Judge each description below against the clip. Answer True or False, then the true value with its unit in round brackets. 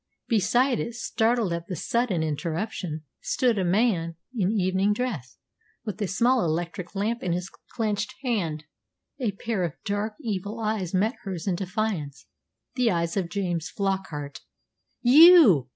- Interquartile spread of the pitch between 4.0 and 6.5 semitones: True (4.7 semitones)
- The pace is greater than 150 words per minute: False (145 wpm)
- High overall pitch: True (195 Hz)